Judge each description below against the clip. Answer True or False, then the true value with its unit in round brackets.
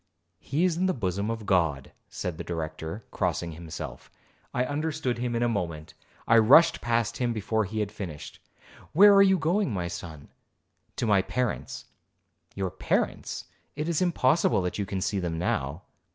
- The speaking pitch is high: False (110 Hz)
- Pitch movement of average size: False (7.7 semitones)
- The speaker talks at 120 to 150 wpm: False (165 wpm)